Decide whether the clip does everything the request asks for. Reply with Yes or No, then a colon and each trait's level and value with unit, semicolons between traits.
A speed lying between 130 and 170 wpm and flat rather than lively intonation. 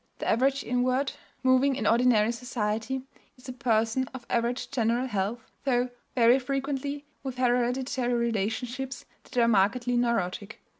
Yes: slow, 135 wpm; narrow, 2.0 semitones